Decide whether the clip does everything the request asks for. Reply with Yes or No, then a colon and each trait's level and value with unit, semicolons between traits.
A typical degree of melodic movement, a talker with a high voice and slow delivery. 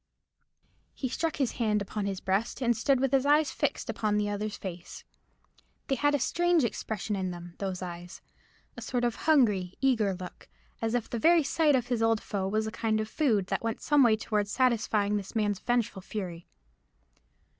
No: average, 4.3 semitones; high, 220 Hz; average, 190 wpm